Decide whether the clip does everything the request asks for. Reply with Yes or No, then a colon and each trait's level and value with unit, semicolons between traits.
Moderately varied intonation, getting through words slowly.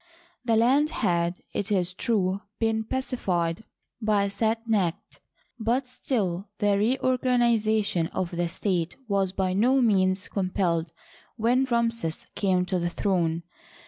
Yes: average, 4.2 semitones; slow, 130 wpm